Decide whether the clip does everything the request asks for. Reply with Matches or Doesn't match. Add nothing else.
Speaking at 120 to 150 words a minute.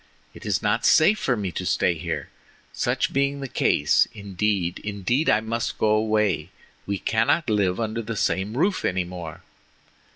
Doesn't match